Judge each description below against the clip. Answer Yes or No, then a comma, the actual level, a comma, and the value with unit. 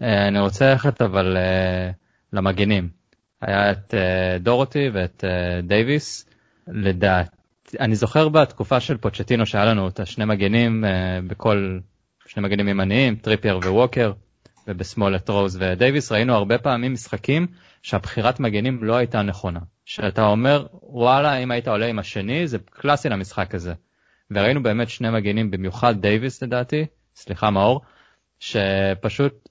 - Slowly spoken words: No, average, 135 wpm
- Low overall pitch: Yes, low, 105 Hz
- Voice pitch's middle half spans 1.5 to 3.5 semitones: No, average, 4.0 semitones